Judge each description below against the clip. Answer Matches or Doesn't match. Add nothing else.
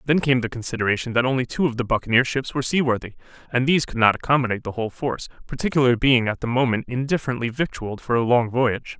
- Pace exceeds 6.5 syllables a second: Matches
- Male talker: Matches